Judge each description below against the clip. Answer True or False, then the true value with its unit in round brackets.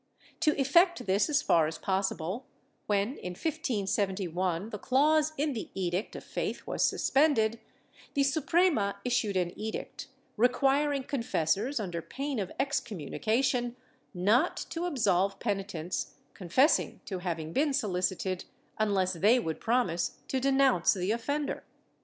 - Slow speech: True (130 wpm)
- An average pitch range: False (6.6 semitones)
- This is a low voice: False (220 Hz)